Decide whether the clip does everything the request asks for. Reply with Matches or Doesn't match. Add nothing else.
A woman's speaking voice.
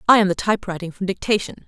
Matches